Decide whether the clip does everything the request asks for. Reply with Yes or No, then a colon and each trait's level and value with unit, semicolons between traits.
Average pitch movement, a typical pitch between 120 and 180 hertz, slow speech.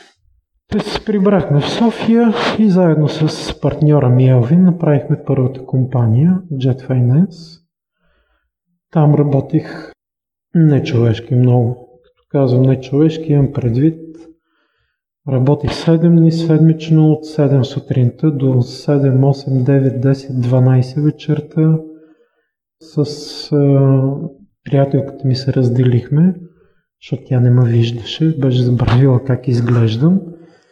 Yes: average, 3.7 semitones; medium, 140 Hz; slow, 110 wpm